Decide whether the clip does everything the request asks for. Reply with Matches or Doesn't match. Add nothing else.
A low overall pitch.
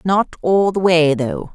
Doesn't match